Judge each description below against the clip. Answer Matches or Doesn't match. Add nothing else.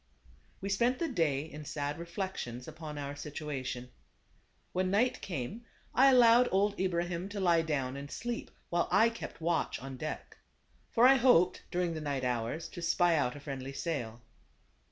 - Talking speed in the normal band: Matches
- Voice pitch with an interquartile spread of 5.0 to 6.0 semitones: Matches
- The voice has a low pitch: Doesn't match